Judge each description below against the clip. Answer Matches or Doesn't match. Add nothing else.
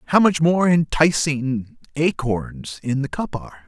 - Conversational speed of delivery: Matches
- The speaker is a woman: Doesn't match